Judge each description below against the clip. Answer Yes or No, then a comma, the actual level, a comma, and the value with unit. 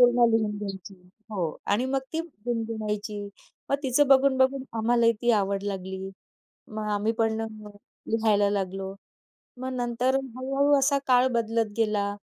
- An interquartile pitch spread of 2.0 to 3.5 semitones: No, average, 3.9 semitones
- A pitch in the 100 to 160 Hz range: No, high, 225 Hz